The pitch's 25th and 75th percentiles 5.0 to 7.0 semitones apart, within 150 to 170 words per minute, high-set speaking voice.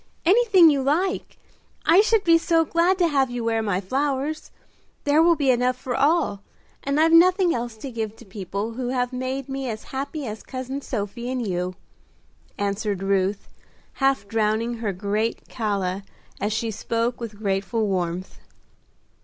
Yes: wide, 5.4 semitones; average, 160 wpm; high, 245 Hz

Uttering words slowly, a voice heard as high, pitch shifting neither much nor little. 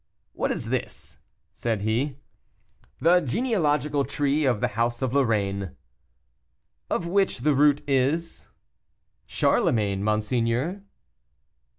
No: slow, 100 wpm; low, 135 Hz; average, 4.9 semitones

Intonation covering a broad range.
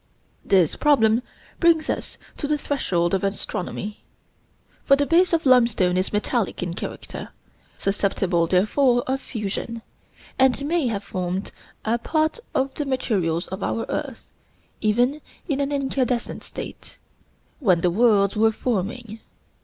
Yes: wide, 5.8 semitones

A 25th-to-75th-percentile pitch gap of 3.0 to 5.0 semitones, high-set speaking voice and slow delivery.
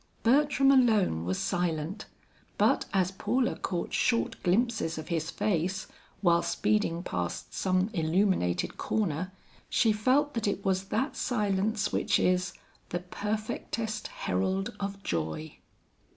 Yes: average, 4.4 semitones; high, 195 Hz; slow, 125 wpm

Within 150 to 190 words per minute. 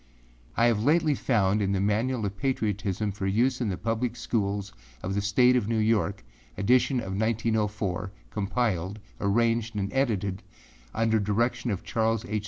Yes: average, 160 wpm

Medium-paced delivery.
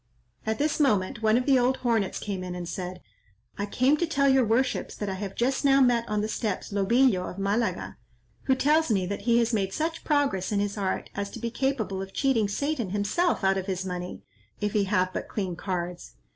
No: fast, 220 wpm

